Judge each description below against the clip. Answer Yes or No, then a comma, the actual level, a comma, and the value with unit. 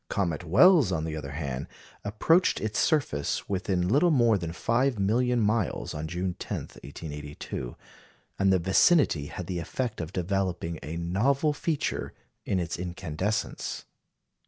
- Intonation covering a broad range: Yes, wide, 6.0 semitones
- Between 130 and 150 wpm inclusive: Yes, average, 140 wpm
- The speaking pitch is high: No, very low, 95 Hz